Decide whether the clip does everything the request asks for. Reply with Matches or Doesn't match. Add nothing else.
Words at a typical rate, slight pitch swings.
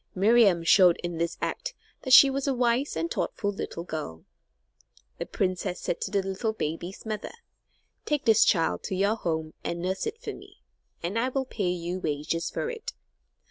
Doesn't match